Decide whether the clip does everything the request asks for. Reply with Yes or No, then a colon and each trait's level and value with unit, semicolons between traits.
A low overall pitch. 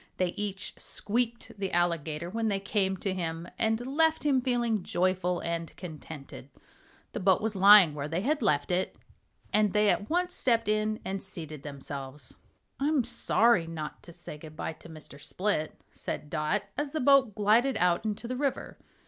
No: high, 195 Hz